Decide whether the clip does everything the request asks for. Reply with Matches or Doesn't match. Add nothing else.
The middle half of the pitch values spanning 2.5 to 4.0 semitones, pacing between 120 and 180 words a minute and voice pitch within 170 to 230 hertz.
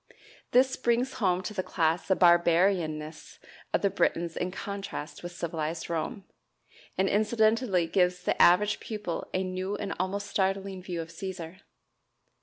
Matches